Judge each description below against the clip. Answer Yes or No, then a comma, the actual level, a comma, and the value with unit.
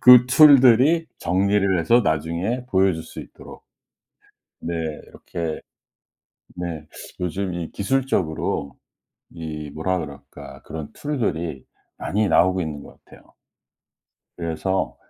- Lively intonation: Yes, wide, 6.2 semitones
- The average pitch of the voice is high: No, very low, 90 Hz